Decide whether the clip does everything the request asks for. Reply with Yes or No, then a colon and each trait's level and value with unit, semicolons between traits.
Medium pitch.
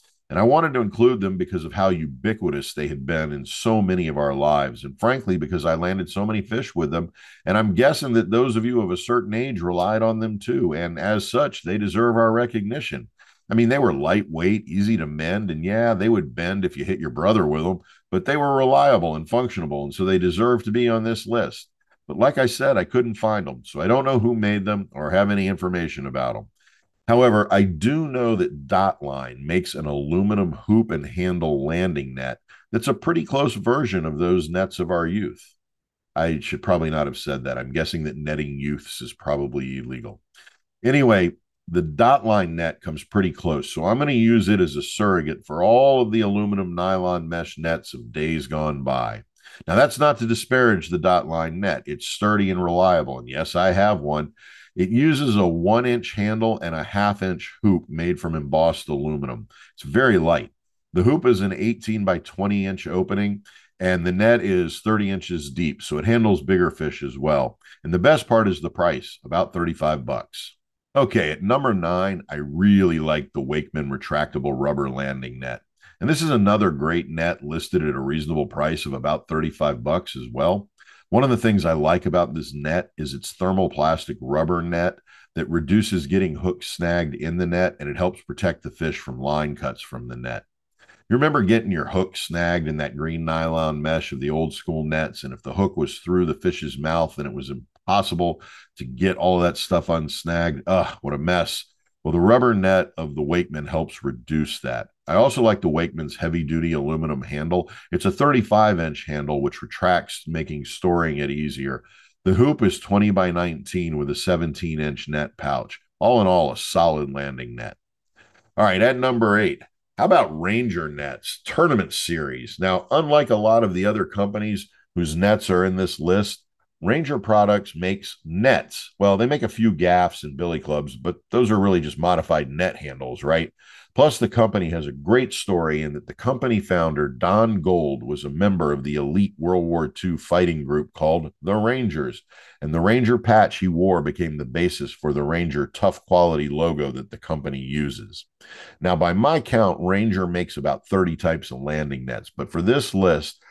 No: very low, 90 Hz